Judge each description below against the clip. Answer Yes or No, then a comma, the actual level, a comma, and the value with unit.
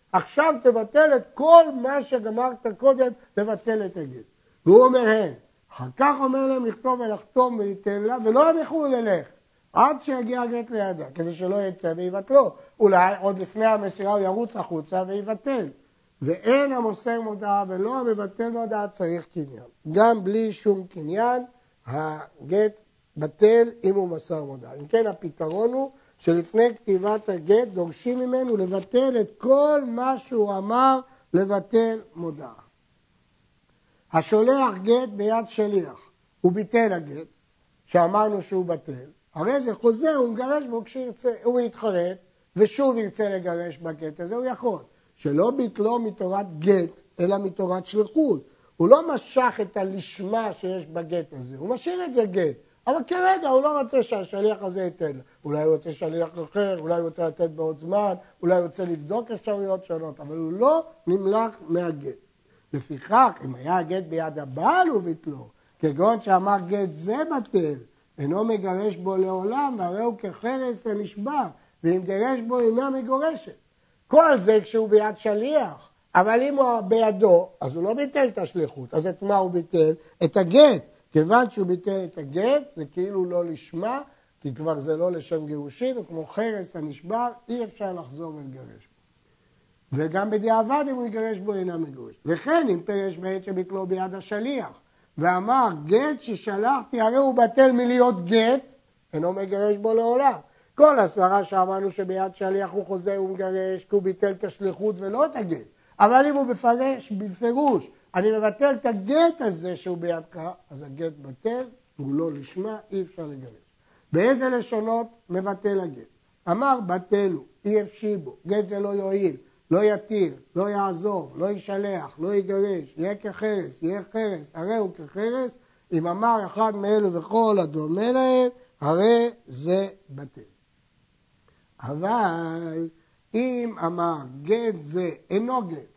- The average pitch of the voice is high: Yes, high, 205 Hz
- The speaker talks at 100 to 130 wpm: No, average, 145 wpm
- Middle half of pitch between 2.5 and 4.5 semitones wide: No, average, 5.2 semitones